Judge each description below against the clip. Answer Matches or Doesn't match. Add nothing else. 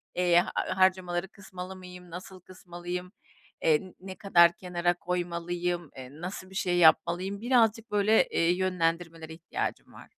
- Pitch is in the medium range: Matches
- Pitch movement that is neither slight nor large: Doesn't match